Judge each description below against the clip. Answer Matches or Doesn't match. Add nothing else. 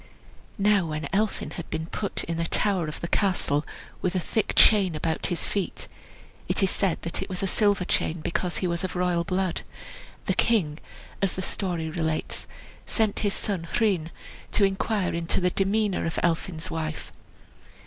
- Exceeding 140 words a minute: Matches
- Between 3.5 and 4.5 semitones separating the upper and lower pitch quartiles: Doesn't match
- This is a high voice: Doesn't match